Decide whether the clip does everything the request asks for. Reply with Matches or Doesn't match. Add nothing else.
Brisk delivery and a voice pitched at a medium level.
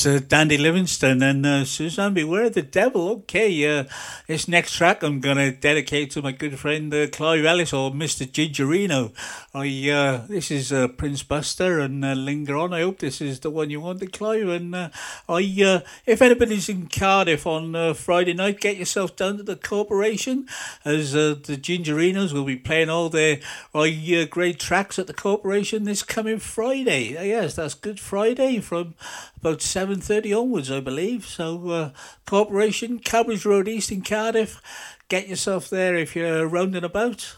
Doesn't match